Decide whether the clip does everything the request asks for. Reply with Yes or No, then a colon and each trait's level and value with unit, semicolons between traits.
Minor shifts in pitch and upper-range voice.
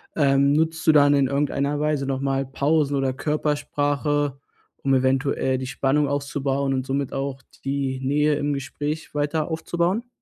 No: narrow, 1.5 semitones; medium, 140 Hz